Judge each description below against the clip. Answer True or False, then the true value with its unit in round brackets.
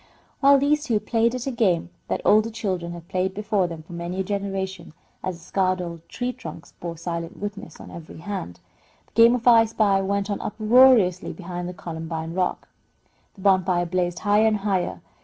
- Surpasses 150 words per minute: True (190 wpm)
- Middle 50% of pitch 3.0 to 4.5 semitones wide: True (3.8 semitones)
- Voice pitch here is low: False (190 Hz)